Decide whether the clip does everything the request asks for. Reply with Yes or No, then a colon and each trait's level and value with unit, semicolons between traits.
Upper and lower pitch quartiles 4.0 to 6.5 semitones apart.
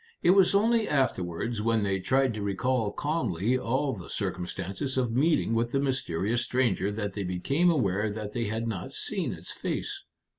Yes: average, 4.9 semitones